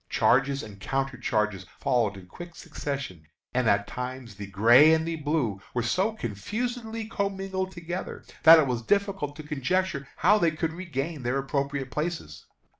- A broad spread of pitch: Yes, wide, 6.4 semitones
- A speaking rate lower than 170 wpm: Yes, average, 160 wpm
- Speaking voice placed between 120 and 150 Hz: Yes, medium, 140 Hz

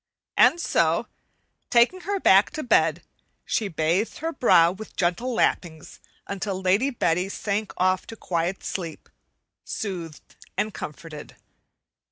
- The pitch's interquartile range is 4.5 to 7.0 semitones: Yes, average, 5.1 semitones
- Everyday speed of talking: No, slow, 125 wpm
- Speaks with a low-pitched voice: No, high, 190 Hz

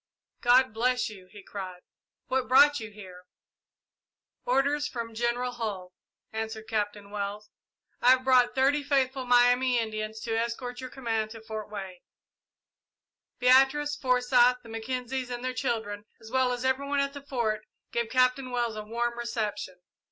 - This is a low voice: No, high, 240 Hz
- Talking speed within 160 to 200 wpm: No, average, 150 wpm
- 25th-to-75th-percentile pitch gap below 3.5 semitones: Yes, average, 3.0 semitones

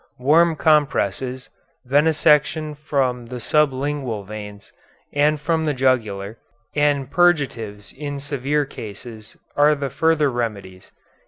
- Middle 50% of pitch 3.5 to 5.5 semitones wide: Yes, average, 4.3 semitones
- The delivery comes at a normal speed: No, slow, 105 wpm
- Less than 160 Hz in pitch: Yes, medium, 140 Hz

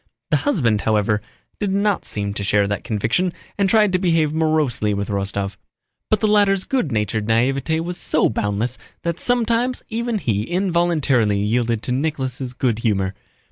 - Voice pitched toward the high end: No, low, 130 Hz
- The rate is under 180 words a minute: Yes, average, 160 wpm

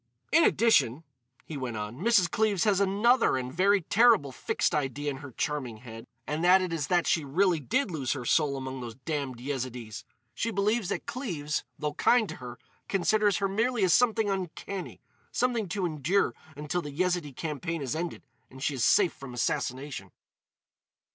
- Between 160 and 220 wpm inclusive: Yes, average, 170 wpm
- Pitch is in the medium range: Yes, medium, 165 Hz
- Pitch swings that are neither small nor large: No, wide, 6.8 semitones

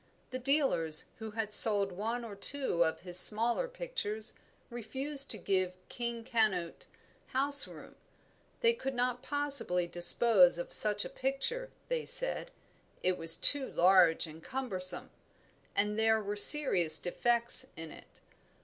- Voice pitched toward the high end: Yes, high, 220 Hz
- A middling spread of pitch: No, wide, 6.5 semitones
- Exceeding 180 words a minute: No, average, 140 wpm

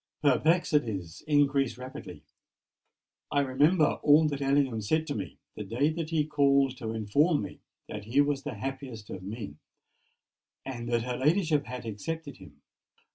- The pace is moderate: Yes, average, 150 wpm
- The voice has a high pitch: No, low, 135 Hz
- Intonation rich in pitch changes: No, average, 4.8 semitones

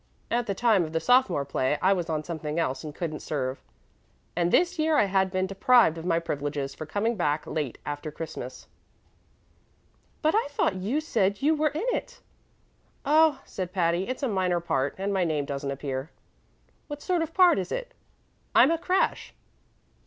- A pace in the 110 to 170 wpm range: No, average, 190 wpm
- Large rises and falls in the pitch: Yes, wide, 8.9 semitones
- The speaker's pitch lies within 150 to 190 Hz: Yes, medium, 185 Hz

